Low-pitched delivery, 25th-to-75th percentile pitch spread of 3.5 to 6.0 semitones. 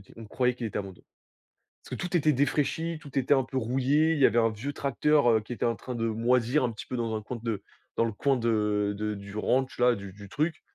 Yes: low, 120 Hz; average, 4.1 semitones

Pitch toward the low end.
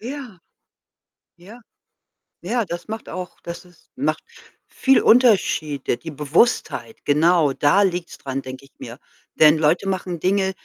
No: medium, 175 Hz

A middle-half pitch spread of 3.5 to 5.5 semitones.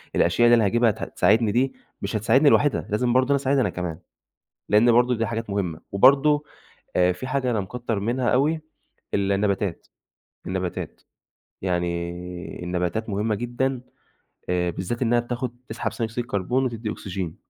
Yes: average, 4.6 semitones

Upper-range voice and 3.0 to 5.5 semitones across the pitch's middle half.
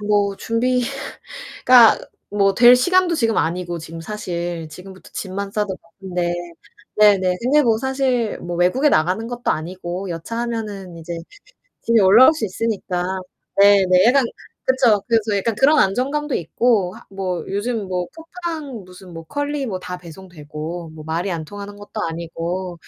Yes: high, 200 Hz; average, 5.1 semitones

